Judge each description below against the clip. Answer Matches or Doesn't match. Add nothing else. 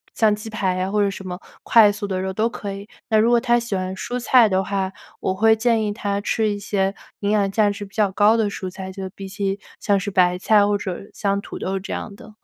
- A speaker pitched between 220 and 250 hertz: Doesn't match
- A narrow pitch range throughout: Matches